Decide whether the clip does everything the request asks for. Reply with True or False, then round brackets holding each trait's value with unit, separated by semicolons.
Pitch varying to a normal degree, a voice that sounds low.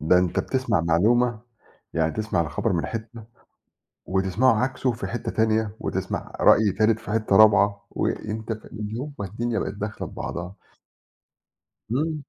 True (3.2 semitones; 110 Hz)